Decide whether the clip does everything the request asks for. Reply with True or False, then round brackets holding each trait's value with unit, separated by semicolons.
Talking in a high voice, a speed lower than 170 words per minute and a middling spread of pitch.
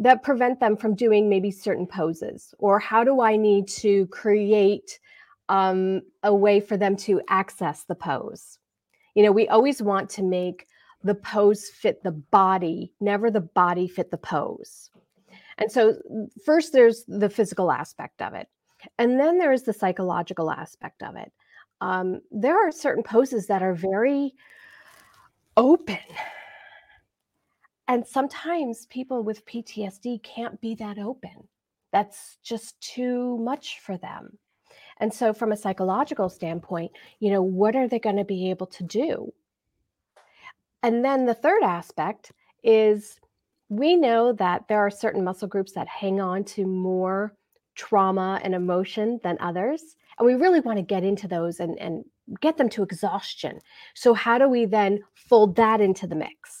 True (210 Hz; 155 wpm; 4.2 semitones)